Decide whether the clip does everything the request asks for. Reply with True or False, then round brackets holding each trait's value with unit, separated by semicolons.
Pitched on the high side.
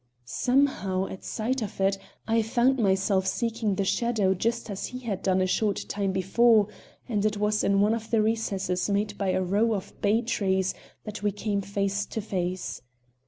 True (205 Hz)